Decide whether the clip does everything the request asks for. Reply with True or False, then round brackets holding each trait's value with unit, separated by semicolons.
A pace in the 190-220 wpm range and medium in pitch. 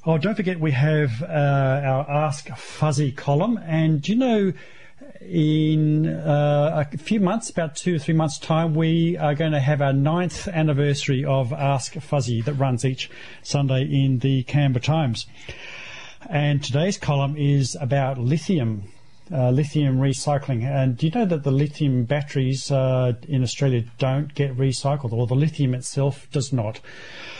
False (160 wpm; 145 Hz)